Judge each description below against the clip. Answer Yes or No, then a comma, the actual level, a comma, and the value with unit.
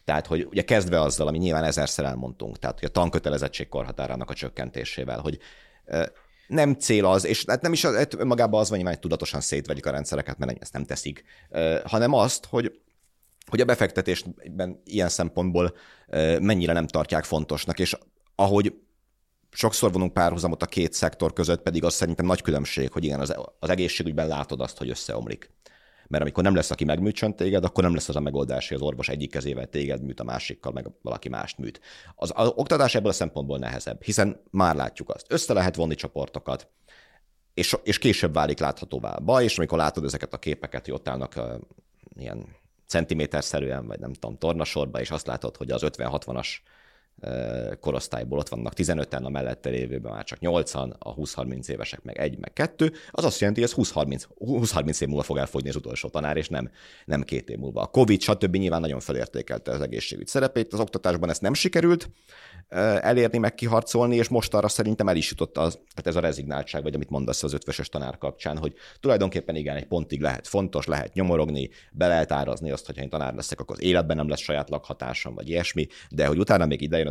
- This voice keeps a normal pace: No, fast, 190 wpm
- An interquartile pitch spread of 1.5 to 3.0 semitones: No, average, 4.9 semitones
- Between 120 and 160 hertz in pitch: No, very low, 80 Hz